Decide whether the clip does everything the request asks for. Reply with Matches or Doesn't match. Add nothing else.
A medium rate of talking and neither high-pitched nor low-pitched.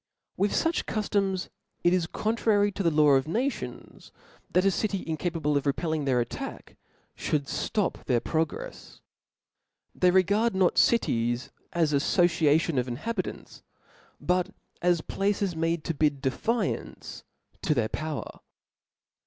Doesn't match